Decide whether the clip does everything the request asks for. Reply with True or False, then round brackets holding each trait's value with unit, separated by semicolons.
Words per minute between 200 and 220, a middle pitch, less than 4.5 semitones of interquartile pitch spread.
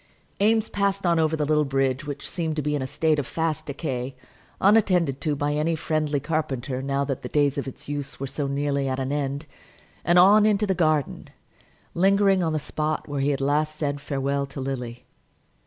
True (205 wpm; 145 Hz; 2.9 semitones)